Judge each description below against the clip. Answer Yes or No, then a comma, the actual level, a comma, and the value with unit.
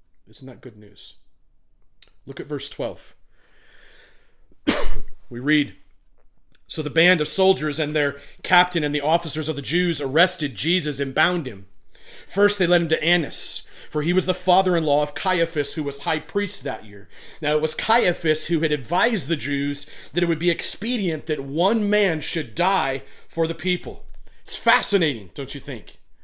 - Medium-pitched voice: Yes, medium, 155 Hz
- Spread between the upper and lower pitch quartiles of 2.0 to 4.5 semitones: Yes, average, 3.9 semitones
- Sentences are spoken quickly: No, average, 175 wpm